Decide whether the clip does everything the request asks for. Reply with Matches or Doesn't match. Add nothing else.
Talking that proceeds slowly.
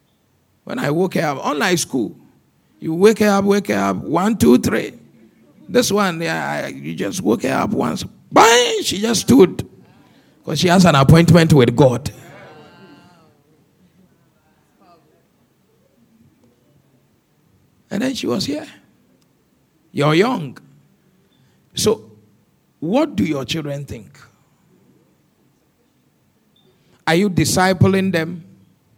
Matches